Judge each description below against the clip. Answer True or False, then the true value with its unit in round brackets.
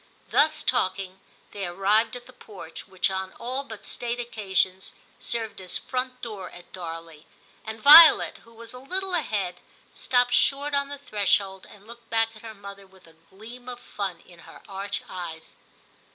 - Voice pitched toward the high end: True (215 Hz)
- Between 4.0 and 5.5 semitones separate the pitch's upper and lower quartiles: True (4.5 semitones)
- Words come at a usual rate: True (170 wpm)